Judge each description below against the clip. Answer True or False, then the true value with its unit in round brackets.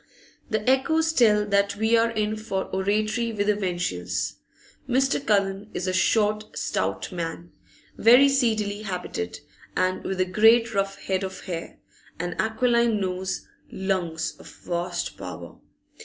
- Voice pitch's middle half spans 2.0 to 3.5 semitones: True (3.2 semitones)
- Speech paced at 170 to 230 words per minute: False (135 wpm)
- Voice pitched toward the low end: False (200 Hz)